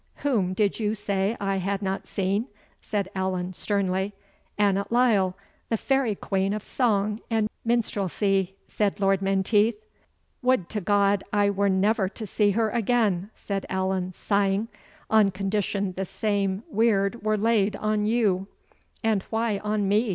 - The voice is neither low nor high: No, high, 200 Hz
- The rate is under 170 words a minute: Yes, average, 145 wpm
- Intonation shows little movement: Yes, narrow, 2.0 semitones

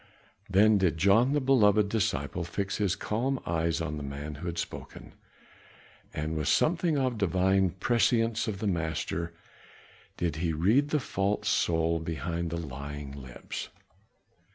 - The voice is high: No, very low, 90 Hz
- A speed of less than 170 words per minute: Yes, average, 145 wpm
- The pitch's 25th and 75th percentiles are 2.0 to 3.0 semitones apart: No, average, 5.0 semitones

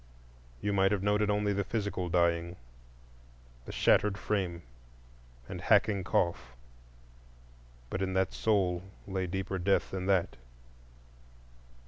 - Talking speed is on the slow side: Yes, slow, 115 wpm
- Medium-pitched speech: No, very low, 95 Hz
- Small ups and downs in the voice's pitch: Yes, narrow, 2.3 semitones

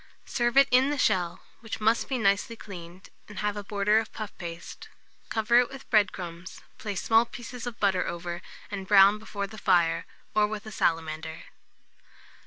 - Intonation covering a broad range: No, average, 3.7 semitones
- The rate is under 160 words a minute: No, average, 180 wpm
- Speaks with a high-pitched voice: Yes, high, 205 Hz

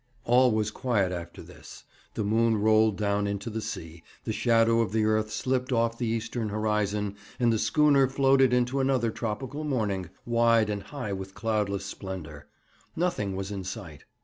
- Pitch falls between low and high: No, low, 110 Hz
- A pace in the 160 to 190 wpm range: Yes, average, 170 wpm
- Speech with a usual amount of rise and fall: Yes, average, 3.1 semitones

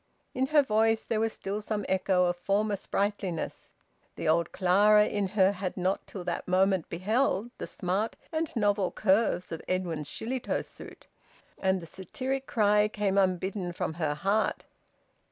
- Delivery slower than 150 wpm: No, average, 155 wpm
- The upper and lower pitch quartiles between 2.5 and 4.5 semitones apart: Yes, average, 2.8 semitones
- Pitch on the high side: Yes, high, 195 Hz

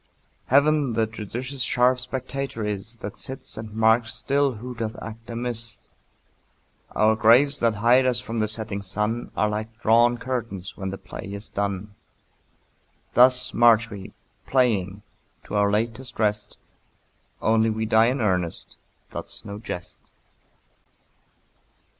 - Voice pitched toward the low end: Yes, low, 115 Hz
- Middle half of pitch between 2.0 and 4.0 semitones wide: Yes, average, 2.8 semitones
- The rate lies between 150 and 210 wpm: No, slow, 135 wpm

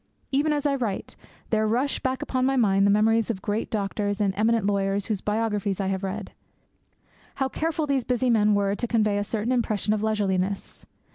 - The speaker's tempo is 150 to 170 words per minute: No, average, 200 wpm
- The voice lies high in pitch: Yes, high, 215 Hz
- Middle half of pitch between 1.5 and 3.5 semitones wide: Yes, average, 3.2 semitones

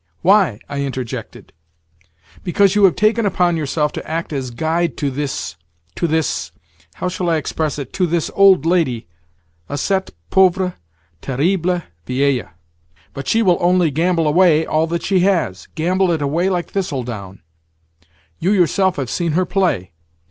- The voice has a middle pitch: Yes, medium, 165 Hz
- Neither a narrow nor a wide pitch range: Yes, average, 4.7 semitones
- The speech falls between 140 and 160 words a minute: Yes, average, 145 wpm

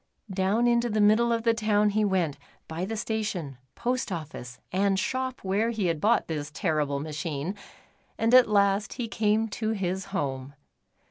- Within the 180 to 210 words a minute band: No, average, 170 wpm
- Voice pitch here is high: Yes, high, 200 Hz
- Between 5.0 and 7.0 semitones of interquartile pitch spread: Yes, wide, 5.4 semitones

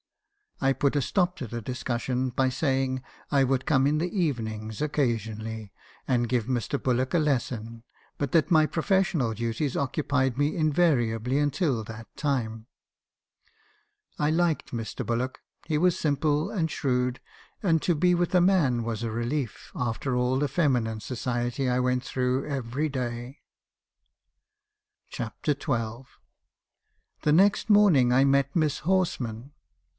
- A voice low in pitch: Yes, low, 130 Hz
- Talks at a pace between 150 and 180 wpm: No, average, 140 wpm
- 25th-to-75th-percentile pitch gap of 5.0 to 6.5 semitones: No, average, 4.1 semitones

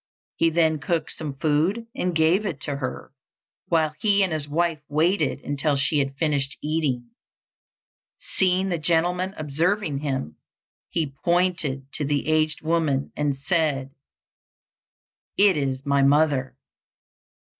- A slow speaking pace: Yes, slow, 130 wpm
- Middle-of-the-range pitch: Yes, medium, 155 Hz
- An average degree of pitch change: Yes, average, 3.3 semitones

